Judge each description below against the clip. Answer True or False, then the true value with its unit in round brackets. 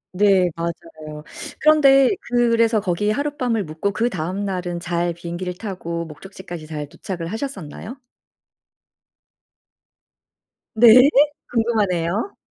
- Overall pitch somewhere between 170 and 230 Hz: True (190 Hz)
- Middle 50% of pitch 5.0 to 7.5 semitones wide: True (5.3 semitones)